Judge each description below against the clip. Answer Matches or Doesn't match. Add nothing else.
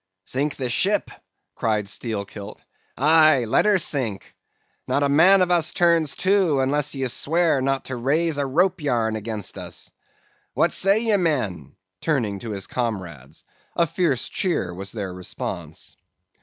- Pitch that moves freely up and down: Matches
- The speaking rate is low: Doesn't match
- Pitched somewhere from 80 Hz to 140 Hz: Matches